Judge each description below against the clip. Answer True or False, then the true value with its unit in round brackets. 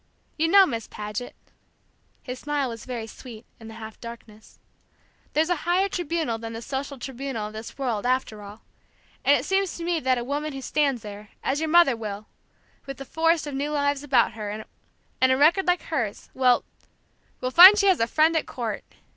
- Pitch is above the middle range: True (265 Hz)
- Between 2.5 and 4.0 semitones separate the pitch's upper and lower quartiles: False (5.5 semitones)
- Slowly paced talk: False (195 wpm)